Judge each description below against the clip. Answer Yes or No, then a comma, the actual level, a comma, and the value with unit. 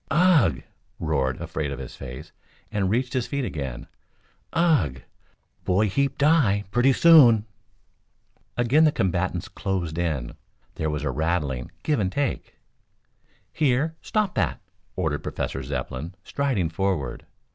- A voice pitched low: Yes, very low, 95 Hz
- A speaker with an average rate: No, slow, 125 wpm